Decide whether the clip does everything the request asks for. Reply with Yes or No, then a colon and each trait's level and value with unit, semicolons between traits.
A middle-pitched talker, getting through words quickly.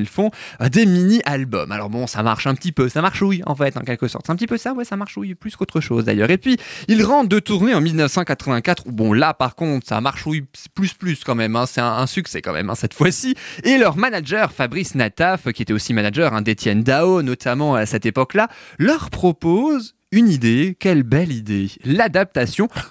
Yes: medium, 150 Hz; fast, 225 wpm